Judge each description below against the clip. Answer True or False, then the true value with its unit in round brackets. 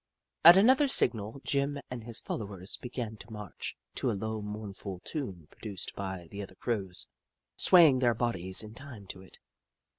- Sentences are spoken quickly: False (160 wpm)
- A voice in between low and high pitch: False (110 Hz)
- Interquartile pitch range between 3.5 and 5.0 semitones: True (4.6 semitones)